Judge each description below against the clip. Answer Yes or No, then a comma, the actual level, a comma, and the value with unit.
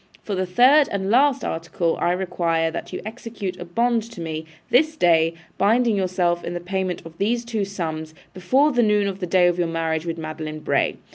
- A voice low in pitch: No, medium, 185 Hz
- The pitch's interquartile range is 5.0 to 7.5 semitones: Yes, average, 5.3 semitones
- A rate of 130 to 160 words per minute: No, average, 200 wpm